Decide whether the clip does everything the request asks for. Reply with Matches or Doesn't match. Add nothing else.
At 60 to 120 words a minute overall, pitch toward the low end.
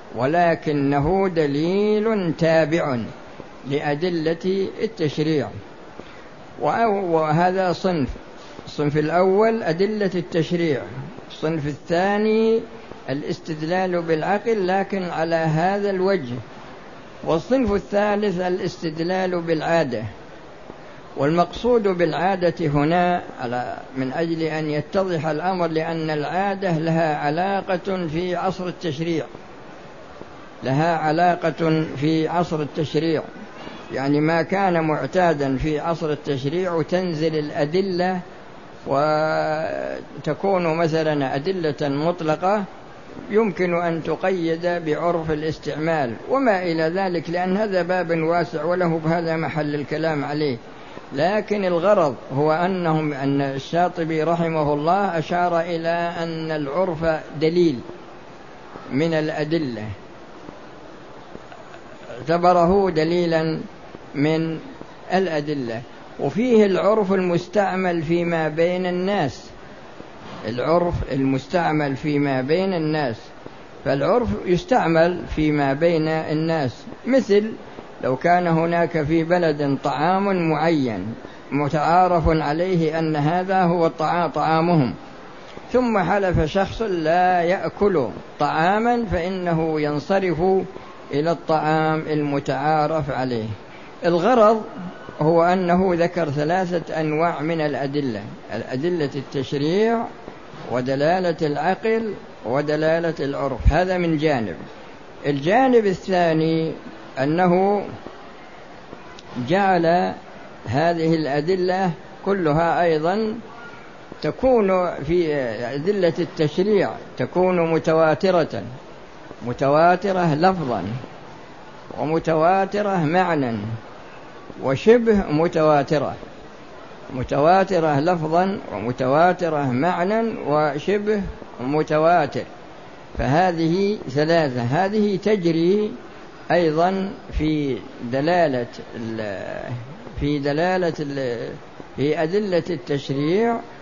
Doesn't match